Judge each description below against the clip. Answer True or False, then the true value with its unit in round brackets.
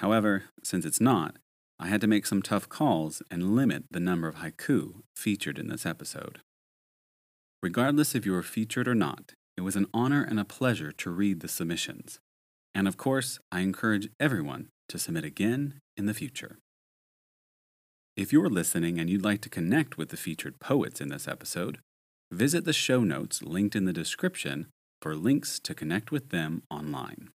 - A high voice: False (105 Hz)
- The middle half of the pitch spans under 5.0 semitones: False (5.6 semitones)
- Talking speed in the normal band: True (180 wpm)